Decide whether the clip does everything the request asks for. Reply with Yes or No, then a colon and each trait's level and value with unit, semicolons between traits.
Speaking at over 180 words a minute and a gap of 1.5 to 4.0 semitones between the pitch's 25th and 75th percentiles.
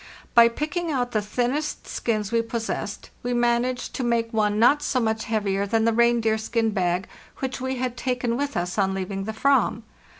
Yes: average, 190 wpm; narrow, 2.6 semitones